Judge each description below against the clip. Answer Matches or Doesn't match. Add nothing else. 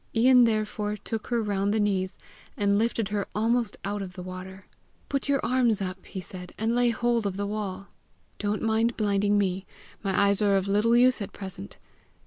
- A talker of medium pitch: Doesn't match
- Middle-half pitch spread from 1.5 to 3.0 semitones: Matches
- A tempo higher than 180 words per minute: Matches